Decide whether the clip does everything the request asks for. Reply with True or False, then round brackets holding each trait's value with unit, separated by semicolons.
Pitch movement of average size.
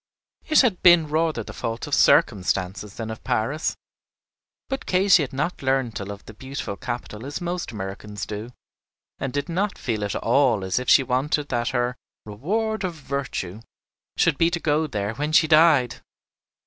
False (6.8 semitones)